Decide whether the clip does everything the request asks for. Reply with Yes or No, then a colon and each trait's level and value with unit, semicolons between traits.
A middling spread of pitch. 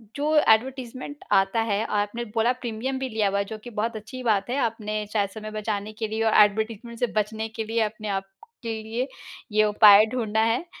No: narrow, 2.0 semitones